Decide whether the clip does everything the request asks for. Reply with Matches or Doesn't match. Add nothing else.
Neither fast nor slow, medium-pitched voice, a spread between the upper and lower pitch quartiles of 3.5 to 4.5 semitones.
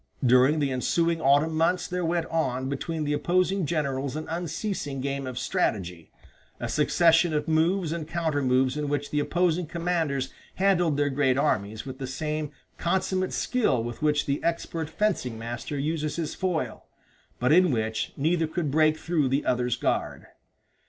Matches